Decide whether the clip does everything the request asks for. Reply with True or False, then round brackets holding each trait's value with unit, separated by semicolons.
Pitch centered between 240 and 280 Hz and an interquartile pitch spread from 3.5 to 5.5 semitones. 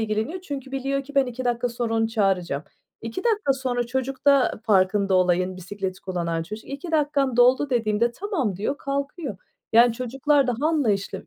True (245 Hz; 5.1 semitones)